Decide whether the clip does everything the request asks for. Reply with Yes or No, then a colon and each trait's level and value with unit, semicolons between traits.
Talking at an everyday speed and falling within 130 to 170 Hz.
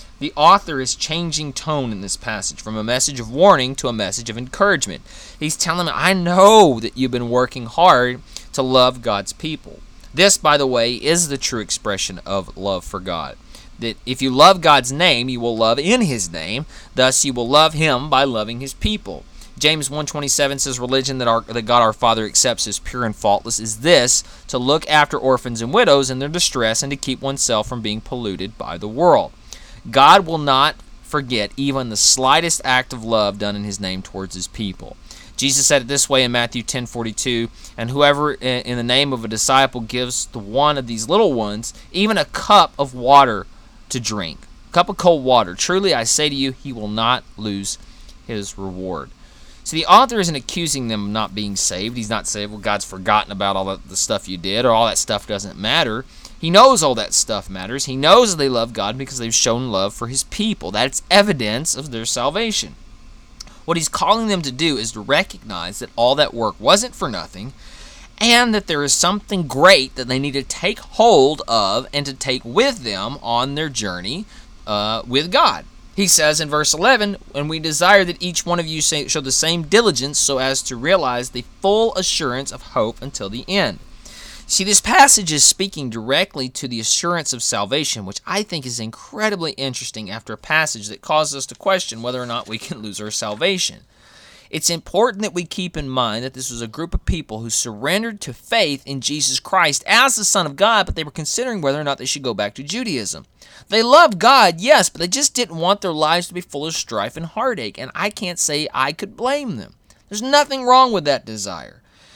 No: fast, 210 wpm; low, 135 Hz